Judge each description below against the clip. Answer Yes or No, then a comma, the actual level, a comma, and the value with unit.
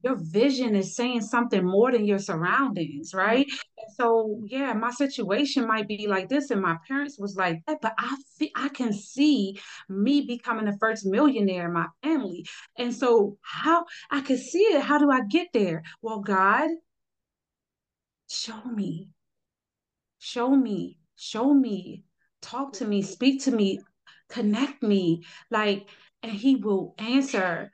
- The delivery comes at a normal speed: Yes, average, 155 wpm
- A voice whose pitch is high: Yes, high, 225 Hz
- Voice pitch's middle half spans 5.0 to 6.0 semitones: Yes, average, 5.3 semitones